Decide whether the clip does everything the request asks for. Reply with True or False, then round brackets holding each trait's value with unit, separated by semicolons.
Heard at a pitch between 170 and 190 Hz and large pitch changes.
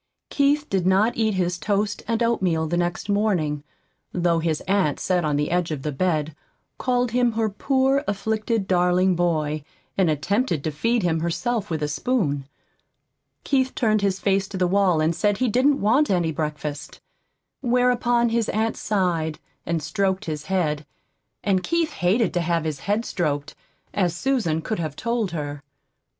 True (185 Hz; 5.8 semitones)